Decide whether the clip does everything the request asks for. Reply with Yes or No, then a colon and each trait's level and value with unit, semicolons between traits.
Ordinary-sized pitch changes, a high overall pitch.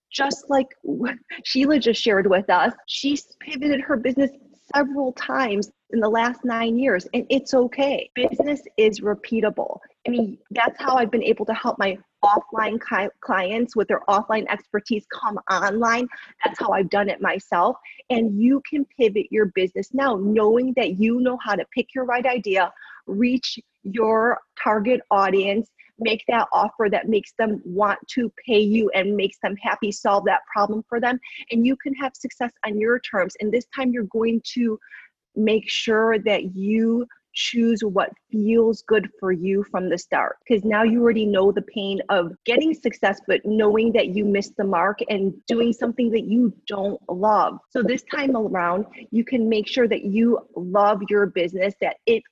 Yes: average, 3.3 semitones; high, 225 Hz